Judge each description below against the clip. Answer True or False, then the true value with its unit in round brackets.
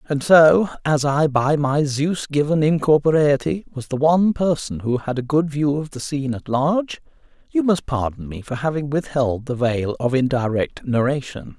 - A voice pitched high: False (140 Hz)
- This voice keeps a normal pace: True (180 wpm)